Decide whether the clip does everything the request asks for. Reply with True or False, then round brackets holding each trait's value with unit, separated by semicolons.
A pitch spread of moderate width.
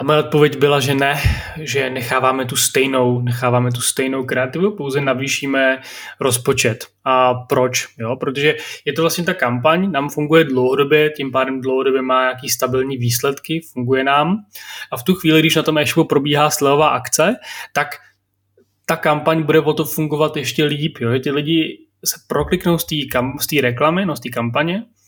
True (3.1 semitones)